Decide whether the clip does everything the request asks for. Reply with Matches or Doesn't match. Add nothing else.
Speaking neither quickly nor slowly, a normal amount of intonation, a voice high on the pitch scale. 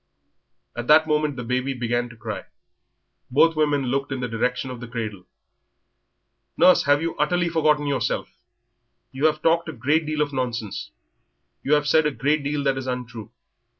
Doesn't match